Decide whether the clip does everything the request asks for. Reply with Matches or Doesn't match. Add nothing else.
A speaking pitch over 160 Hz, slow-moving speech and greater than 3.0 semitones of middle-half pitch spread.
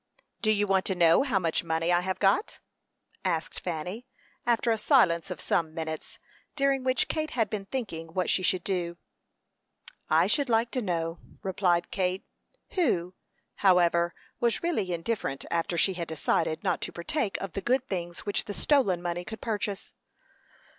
Doesn't match